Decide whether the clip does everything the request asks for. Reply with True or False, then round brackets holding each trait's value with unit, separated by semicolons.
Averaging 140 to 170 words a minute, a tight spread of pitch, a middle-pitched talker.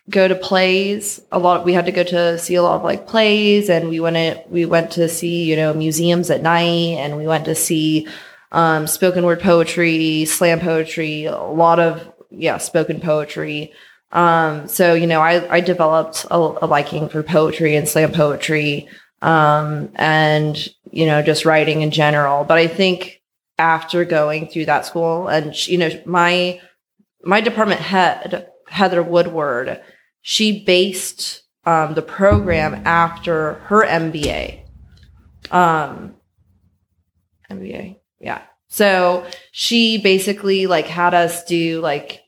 True (150 wpm; 2.3 semitones; 165 Hz)